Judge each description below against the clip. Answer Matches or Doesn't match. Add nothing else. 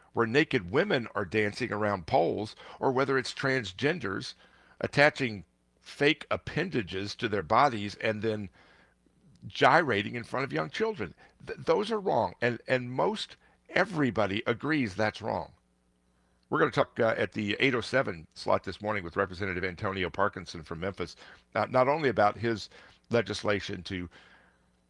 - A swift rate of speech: Doesn't match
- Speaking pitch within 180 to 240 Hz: Doesn't match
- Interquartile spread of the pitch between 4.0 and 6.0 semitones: Matches